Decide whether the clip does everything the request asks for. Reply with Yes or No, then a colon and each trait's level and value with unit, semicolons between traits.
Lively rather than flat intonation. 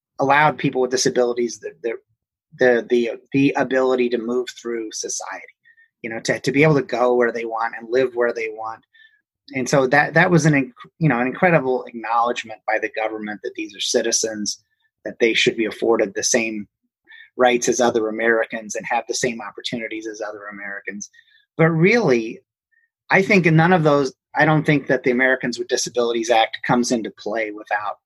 Yes: wide, 5.8 semitones